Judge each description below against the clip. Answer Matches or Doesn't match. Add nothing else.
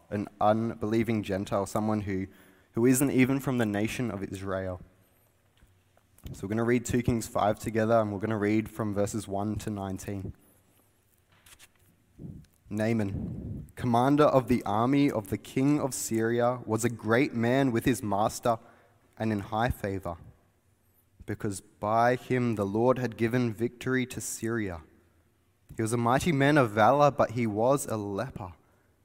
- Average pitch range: Matches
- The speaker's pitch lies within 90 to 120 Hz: Matches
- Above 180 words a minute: Doesn't match